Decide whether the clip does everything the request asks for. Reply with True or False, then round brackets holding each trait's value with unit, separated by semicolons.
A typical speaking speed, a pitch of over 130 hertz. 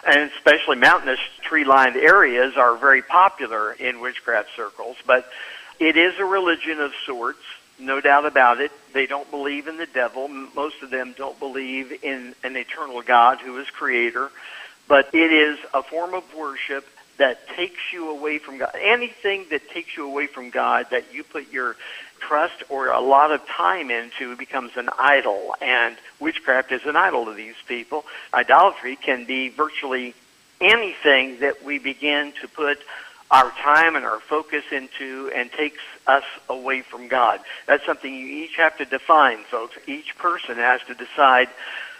True (170 wpm; 140 Hz)